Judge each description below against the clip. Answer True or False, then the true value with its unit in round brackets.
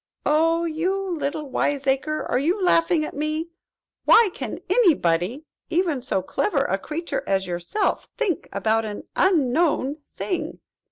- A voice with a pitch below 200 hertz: False (305 Hz)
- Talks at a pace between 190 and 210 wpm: False (145 wpm)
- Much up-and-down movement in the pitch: False (5.0 semitones)